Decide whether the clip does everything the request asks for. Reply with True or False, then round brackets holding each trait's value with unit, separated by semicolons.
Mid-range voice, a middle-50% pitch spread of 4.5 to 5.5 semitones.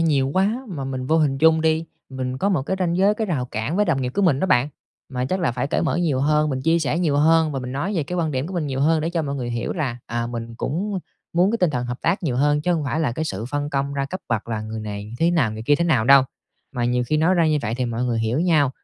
True (145 Hz; 4.8 semitones)